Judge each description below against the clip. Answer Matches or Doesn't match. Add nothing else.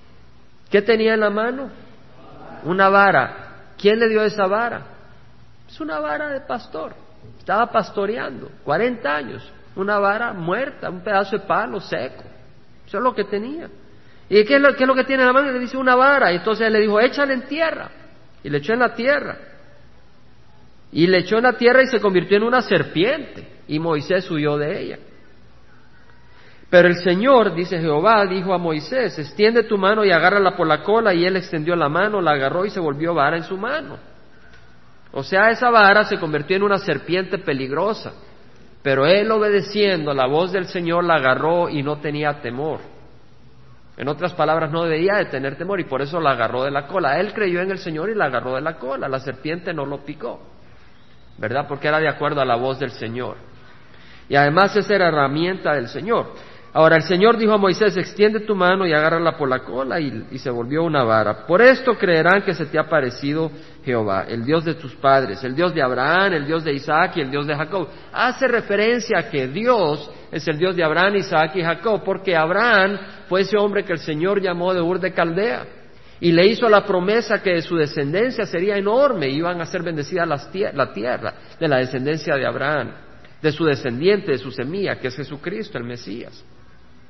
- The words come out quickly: Matches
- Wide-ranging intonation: Matches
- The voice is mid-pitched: Matches